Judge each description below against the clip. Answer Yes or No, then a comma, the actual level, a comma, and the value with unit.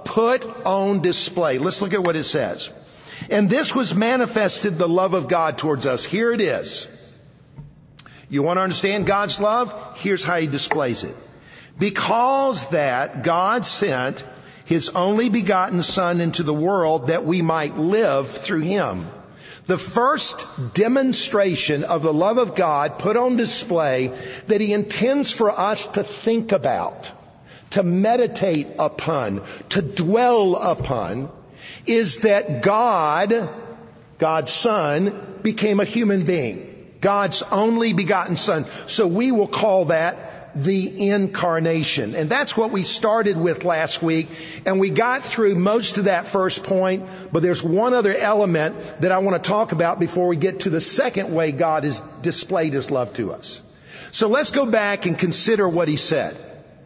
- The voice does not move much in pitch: No, average, 4.4 semitones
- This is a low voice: No, high, 190 Hz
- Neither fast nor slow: Yes, average, 155 wpm